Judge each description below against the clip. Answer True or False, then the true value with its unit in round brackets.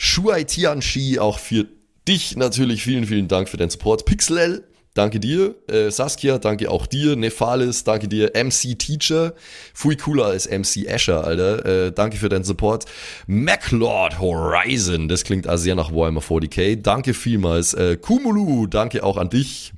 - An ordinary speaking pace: True (155 wpm)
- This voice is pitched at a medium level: False (110 Hz)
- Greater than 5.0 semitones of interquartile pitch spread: True (5.5 semitones)